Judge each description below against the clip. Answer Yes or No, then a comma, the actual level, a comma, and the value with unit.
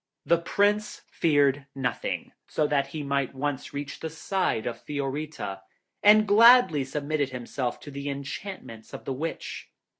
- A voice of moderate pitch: Yes, medium, 145 Hz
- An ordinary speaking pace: Yes, average, 145 wpm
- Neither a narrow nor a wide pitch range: Yes, average, 3.2 semitones